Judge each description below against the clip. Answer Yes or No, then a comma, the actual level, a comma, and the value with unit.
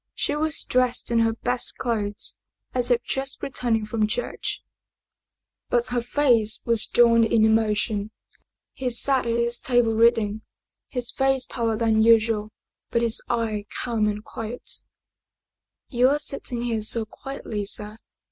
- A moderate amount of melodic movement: No, narrow, 2.1 semitones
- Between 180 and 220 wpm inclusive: No, average, 155 wpm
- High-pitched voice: Yes, high, 230 Hz